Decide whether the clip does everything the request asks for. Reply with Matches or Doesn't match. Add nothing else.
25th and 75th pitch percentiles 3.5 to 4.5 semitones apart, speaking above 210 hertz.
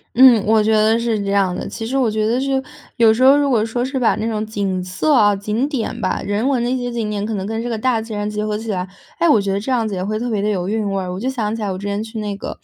Doesn't match